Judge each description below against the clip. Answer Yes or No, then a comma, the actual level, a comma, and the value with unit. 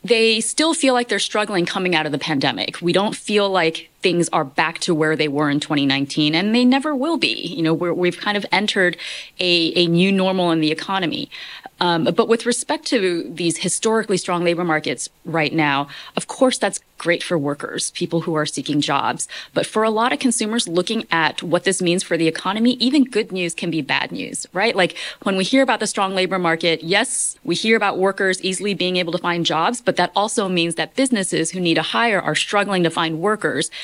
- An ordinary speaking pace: No, fast, 220 wpm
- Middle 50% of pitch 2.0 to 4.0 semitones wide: No, average, 4.7 semitones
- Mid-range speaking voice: Yes, medium, 180 Hz